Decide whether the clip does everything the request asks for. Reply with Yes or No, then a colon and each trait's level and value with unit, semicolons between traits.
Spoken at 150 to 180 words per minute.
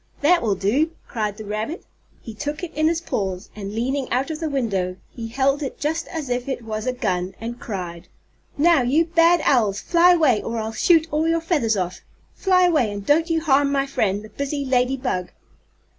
No: fast, 205 wpm